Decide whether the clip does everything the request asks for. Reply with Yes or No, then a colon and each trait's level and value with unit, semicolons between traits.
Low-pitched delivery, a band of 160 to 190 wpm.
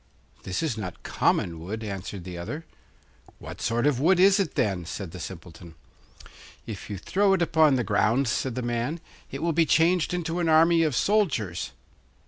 Yes: low, 130 Hz; average, 180 wpm